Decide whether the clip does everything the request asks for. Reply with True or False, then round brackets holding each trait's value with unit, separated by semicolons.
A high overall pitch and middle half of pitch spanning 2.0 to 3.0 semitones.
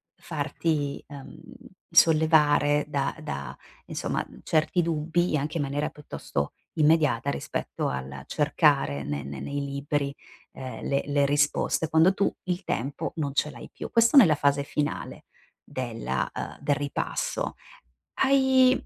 False (145 Hz; 2.6 semitones)